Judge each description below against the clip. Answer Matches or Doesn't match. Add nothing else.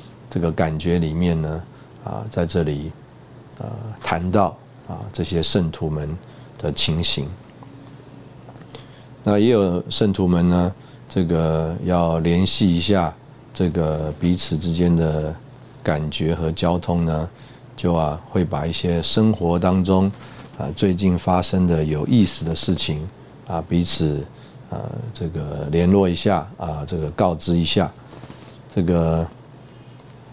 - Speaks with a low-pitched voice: Matches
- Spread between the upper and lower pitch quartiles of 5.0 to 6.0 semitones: Matches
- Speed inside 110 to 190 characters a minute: Matches